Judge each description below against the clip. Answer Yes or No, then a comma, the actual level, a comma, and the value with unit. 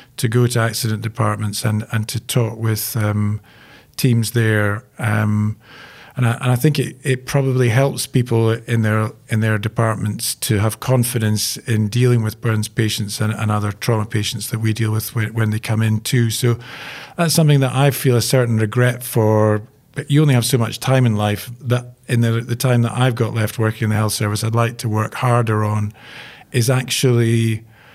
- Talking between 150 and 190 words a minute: No, average, 200 wpm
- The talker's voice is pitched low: Yes, low, 115 Hz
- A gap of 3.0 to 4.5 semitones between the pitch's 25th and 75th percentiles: No, narrow, 2.5 semitones